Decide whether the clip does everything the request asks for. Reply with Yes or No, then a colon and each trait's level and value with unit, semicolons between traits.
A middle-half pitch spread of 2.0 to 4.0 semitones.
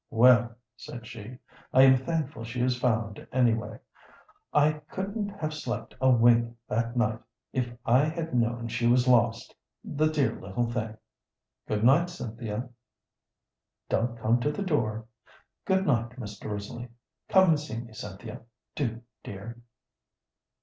Yes: average, 3.3 semitones